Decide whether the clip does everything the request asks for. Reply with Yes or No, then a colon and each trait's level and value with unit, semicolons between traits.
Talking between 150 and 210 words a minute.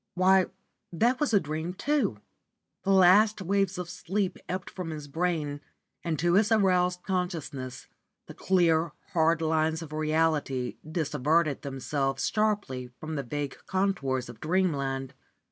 No: slow, 135 wpm